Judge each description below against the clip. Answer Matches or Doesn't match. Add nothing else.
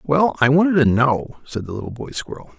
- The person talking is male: Matches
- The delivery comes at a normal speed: Doesn't match